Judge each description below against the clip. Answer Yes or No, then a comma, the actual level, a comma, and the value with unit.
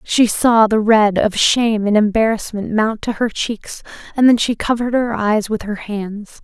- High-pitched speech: Yes, high, 220 Hz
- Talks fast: No, average, 195 wpm